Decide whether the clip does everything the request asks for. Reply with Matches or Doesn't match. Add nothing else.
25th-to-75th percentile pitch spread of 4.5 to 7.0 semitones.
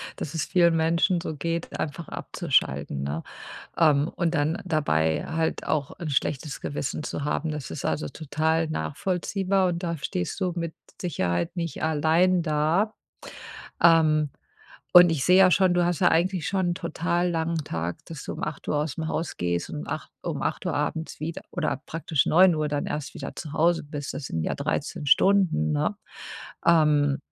Doesn't match